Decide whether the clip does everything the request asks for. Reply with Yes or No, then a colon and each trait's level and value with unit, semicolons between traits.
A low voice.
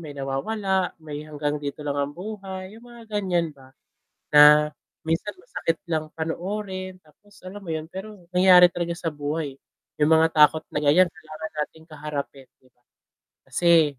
No: medium, 160 Hz